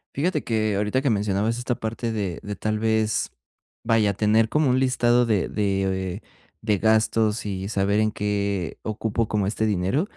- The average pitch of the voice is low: Yes, low, 110 Hz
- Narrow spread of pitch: Yes, narrow, 2.0 semitones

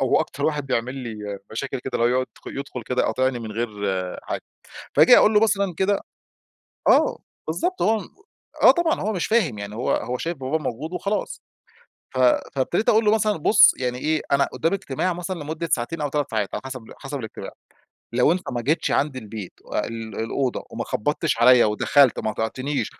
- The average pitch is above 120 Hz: Yes, low, 135 Hz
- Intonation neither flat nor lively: No, wide, 6.1 semitones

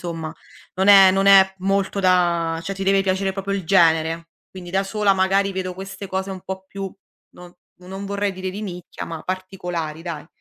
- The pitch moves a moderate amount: No, narrow, 1.7 semitones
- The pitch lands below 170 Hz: No, high, 190 Hz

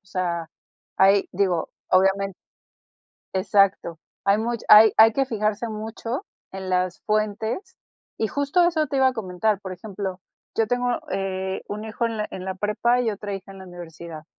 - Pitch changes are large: No, average, 2.9 semitones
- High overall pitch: Yes, high, 205 Hz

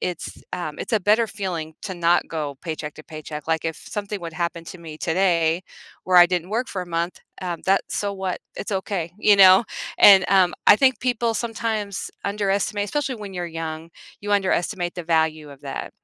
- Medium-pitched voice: Yes, medium, 180 Hz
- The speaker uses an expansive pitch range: No, average, 3.7 semitones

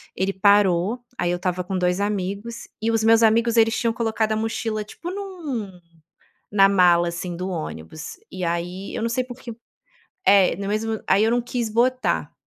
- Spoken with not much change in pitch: No, average, 3.9 semitones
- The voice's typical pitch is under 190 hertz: No, high, 210 Hz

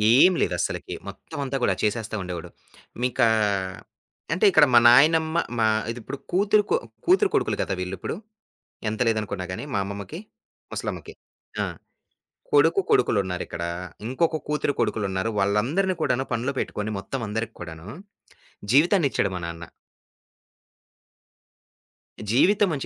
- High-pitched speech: No, low, 120 Hz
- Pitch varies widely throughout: Yes, wide, 8.4 semitones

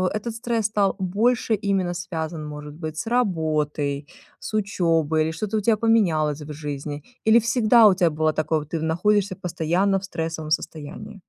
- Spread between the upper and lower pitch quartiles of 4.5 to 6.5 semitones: Yes, average, 5.2 semitones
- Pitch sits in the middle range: Yes, medium, 175 Hz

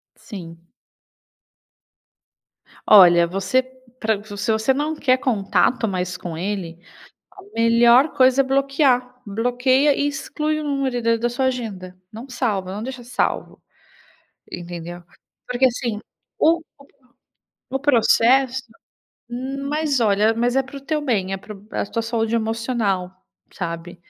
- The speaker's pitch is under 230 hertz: No, high, 235 Hz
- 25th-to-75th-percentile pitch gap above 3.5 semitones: Yes, average, 4.9 semitones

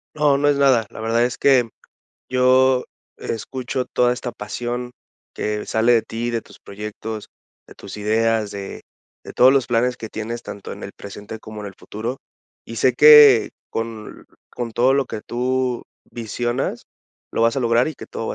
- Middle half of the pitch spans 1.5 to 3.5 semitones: Yes, narrow, 2.4 semitones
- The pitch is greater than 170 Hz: No, low, 120 Hz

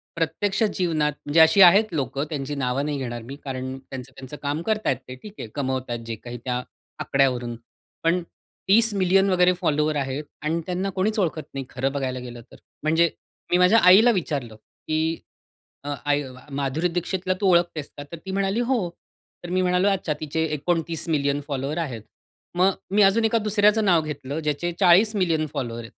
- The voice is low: No, medium, 160 Hz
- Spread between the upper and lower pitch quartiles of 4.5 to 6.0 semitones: Yes, average, 5.3 semitones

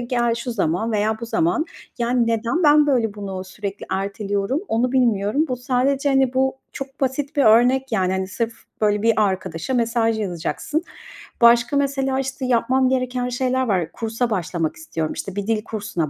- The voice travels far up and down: No, average, 4.2 semitones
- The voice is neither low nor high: No, high, 235 Hz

